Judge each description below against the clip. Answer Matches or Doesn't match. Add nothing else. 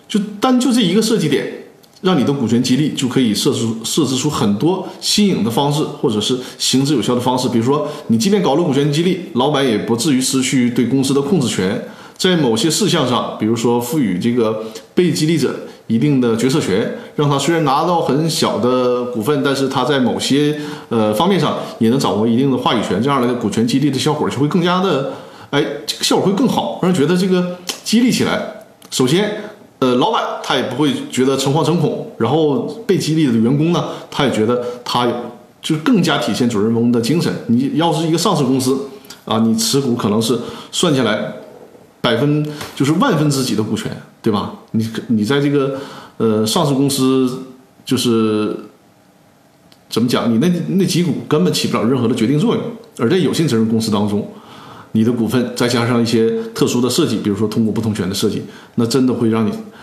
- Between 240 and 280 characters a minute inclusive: Doesn't match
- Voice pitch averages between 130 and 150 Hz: Matches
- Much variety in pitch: Matches